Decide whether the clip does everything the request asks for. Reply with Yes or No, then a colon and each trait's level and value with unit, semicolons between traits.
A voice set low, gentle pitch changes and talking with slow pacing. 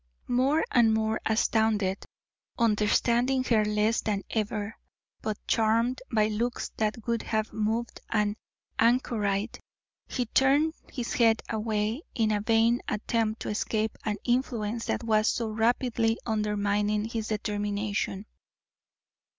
No: high, 220 Hz; narrow, 1.7 semitones; slow, 120 wpm